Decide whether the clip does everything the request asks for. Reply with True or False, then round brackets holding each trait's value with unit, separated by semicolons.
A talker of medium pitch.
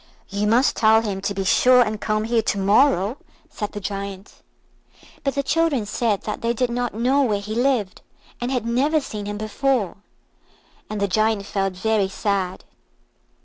False (215 Hz)